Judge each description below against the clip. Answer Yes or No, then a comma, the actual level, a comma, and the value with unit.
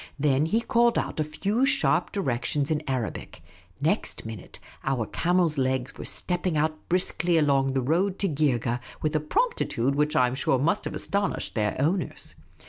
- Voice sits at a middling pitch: Yes, medium, 150 Hz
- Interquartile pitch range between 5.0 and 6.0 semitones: Yes, average, 5.3 semitones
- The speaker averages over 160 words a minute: Yes, average, 170 wpm